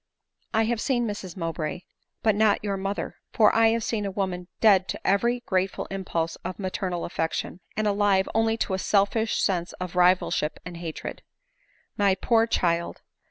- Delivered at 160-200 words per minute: Yes, average, 170 wpm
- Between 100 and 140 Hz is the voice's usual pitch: No, high, 195 Hz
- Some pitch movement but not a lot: Yes, average, 3.3 semitones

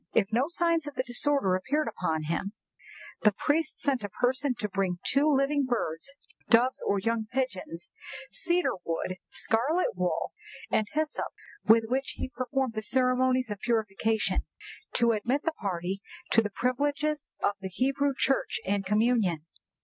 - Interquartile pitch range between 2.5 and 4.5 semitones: No, wide, 5.5 semitones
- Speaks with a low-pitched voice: No, high, 240 Hz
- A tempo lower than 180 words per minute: Yes, average, 150 wpm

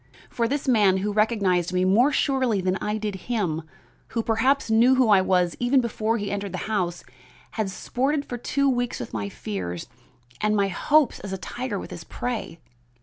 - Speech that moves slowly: No, average, 185 wpm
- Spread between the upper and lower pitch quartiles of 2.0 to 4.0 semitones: No, average, 4.6 semitones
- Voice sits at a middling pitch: No, high, 215 Hz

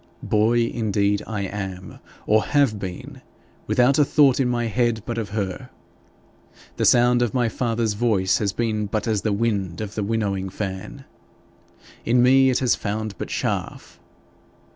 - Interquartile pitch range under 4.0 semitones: Yes, average, 3.0 semitones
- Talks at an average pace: Yes, average, 160 wpm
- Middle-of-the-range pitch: No, low, 110 Hz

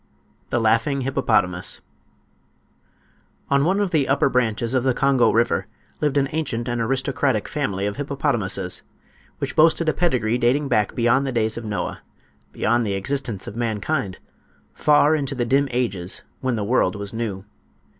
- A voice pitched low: Yes, low, 120 Hz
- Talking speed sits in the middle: Yes, average, 150 wpm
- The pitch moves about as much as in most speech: Yes, average, 4.2 semitones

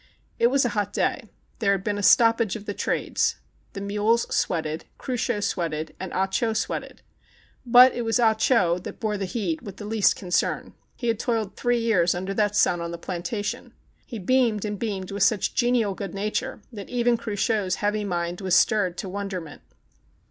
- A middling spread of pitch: Yes, average, 3.5 semitones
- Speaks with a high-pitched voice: Yes, high, 205 Hz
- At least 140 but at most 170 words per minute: No, average, 190 wpm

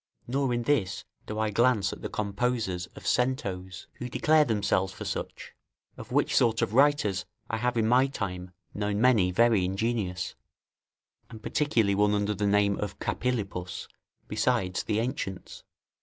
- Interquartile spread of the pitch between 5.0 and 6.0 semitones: No, average, 4.1 semitones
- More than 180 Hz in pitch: No, low, 105 Hz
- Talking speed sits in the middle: Yes, average, 155 wpm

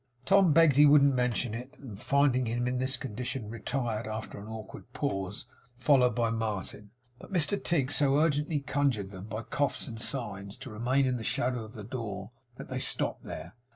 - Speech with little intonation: No, average, 4.2 semitones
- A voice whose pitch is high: No, low, 125 Hz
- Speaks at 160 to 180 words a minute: No, average, 190 wpm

